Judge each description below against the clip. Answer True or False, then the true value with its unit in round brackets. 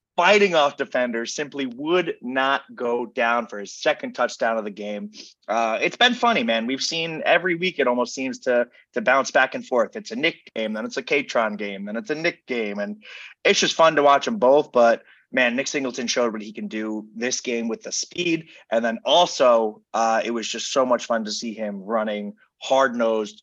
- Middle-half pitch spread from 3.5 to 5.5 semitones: True (4.3 semitones)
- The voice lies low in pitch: True (115 Hz)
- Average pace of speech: False (215 wpm)